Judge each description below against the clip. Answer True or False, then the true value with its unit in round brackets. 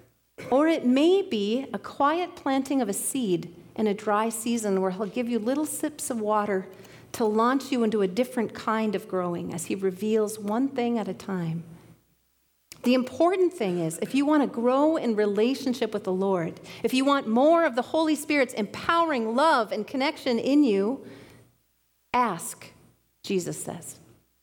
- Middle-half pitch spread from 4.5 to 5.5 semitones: True (5.2 semitones)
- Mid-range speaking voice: False (230 Hz)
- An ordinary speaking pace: True (170 wpm)